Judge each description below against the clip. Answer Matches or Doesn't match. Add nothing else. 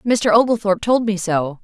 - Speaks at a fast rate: Doesn't match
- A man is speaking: Doesn't match